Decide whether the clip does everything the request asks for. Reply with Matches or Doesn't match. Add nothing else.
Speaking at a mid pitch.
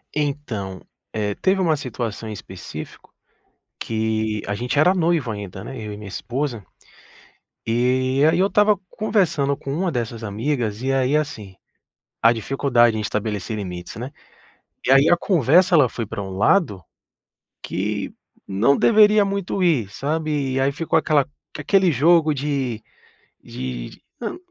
Doesn't match